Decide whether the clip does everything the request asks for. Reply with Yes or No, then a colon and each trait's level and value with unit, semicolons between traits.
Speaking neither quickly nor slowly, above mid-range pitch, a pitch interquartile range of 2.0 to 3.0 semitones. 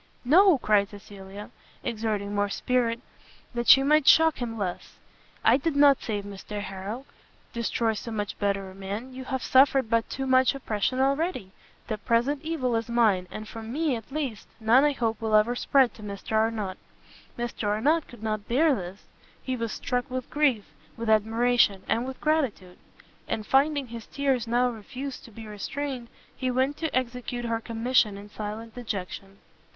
No: average, 175 wpm; high, 235 Hz; average, 3.8 semitones